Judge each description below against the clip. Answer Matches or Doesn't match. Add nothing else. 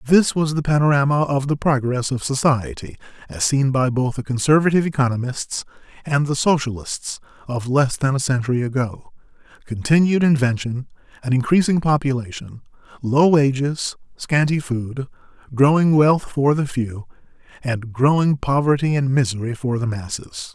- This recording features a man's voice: Matches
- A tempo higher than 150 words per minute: Doesn't match